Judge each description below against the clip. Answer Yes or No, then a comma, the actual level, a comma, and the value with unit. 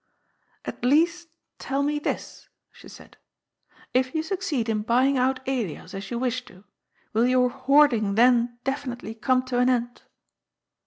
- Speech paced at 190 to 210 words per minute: No, average, 155 wpm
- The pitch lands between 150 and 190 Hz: No, very high, 255 Hz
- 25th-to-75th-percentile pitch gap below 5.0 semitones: Yes, narrow, 2.5 semitones